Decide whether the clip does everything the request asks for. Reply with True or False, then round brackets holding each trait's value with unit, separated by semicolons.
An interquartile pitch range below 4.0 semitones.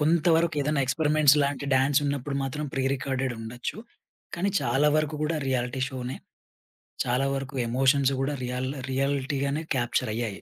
True (2.4 semitones)